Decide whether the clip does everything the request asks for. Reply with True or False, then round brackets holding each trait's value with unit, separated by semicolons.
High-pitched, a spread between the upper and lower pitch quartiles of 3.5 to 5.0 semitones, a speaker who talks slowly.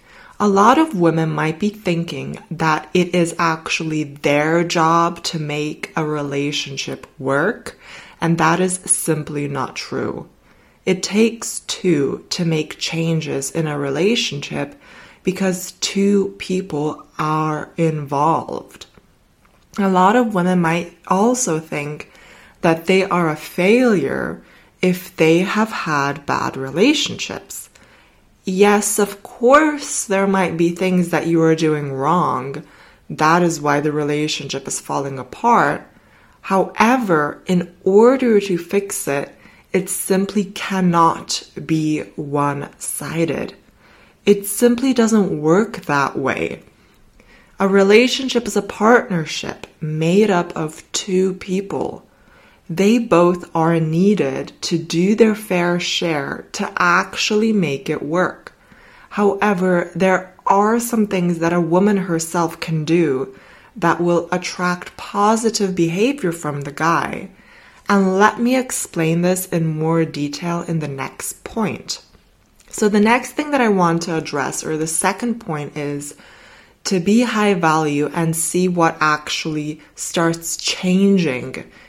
False (175 Hz; 4.0 semitones; 125 wpm)